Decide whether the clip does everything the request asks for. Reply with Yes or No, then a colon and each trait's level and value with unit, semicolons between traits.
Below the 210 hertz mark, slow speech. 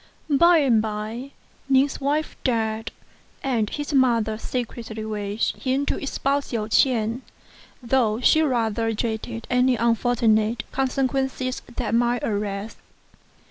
No: high, 235 Hz; slow, 115 wpm